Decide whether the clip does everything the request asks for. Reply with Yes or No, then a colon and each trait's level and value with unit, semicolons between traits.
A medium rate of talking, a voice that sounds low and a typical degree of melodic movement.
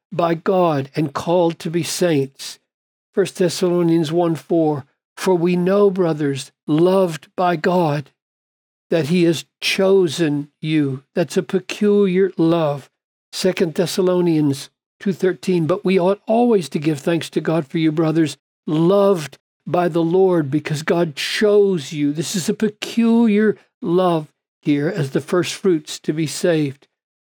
No: average, 145 wpm; medium, 170 Hz; average, 3.5 semitones